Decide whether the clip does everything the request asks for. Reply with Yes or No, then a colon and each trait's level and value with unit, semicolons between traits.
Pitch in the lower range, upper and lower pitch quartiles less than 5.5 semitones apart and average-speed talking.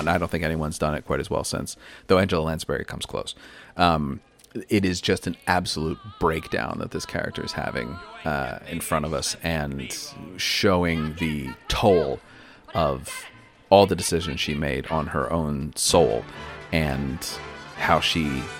Yes: very low, 80 Hz; average, 2.8 semitones; average, 160 wpm